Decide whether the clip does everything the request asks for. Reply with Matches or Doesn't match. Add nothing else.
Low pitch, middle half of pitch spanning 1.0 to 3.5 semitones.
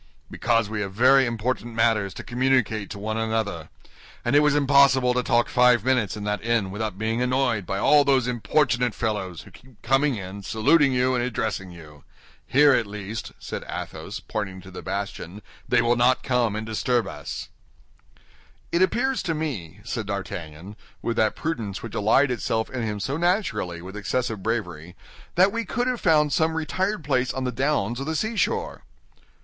Doesn't match